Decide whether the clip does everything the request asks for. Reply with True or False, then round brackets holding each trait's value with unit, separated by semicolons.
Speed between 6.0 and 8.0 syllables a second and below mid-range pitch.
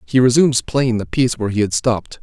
True (6.6 syllables/s; 120 Hz)